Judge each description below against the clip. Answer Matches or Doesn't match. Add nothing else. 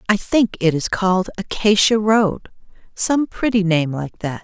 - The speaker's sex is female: Matches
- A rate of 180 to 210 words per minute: Doesn't match